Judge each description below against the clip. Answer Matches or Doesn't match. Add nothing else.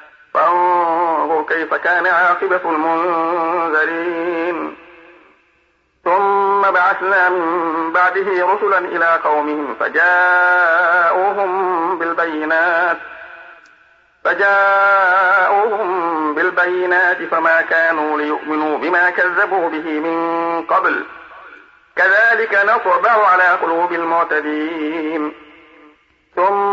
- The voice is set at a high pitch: Doesn't match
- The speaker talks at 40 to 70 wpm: Matches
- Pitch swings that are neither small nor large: Doesn't match